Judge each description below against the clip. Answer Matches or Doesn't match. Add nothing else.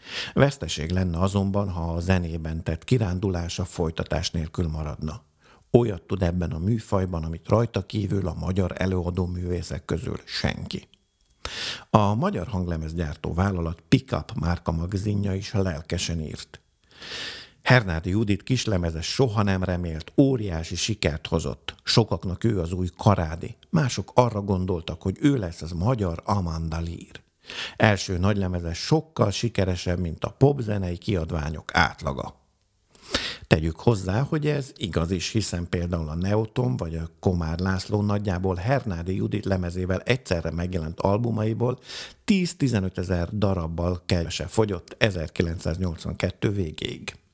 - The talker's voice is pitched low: Matches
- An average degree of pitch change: Matches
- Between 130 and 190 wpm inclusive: Doesn't match